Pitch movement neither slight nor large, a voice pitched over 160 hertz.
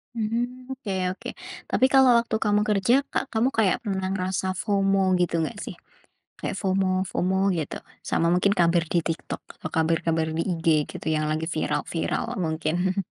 Yes: average, 4.1 semitones; high, 190 Hz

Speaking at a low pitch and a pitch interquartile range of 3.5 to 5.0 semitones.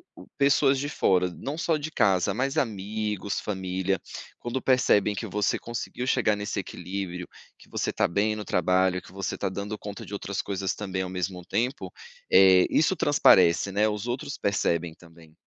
Yes: low, 100 Hz; average, 4.2 semitones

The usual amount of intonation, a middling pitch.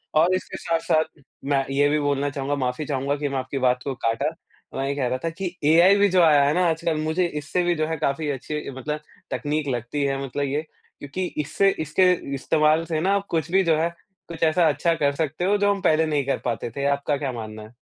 Yes: average, 3.0 semitones; medium, 150 Hz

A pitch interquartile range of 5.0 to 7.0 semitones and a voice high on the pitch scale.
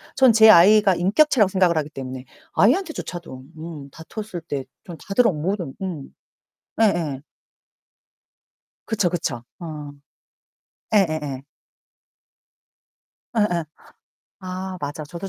No: average, 5.3 semitones; medium, 175 Hz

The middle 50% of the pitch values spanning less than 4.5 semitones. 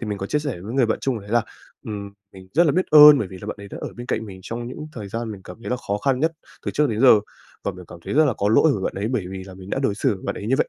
No: average, 5.0 semitones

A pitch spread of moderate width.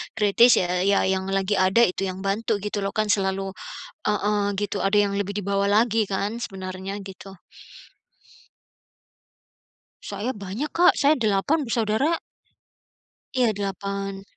No: narrow, 2.1 semitones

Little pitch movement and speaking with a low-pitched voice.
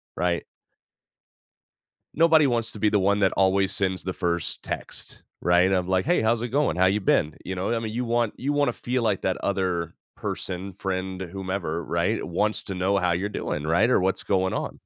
No: average, 3.3 semitones; very low, 95 Hz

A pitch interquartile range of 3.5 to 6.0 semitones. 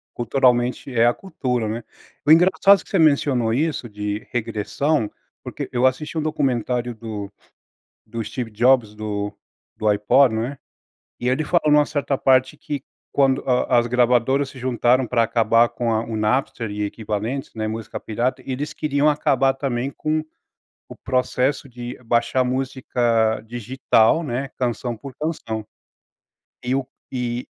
No: average, 3.1 semitones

